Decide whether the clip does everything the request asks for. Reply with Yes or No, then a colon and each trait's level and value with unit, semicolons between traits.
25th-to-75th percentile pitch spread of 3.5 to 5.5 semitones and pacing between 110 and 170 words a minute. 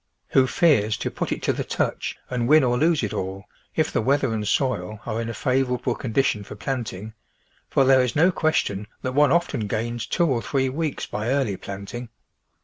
No: average, 4.2 semitones; average, 200 wpm